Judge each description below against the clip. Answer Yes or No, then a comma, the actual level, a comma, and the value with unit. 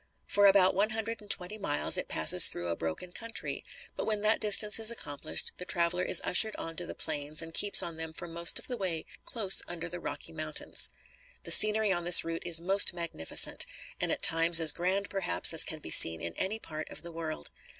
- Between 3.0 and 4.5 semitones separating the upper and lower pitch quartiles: Yes, average, 3.8 semitones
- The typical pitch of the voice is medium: Yes, medium, 175 Hz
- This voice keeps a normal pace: No, fast, 220 wpm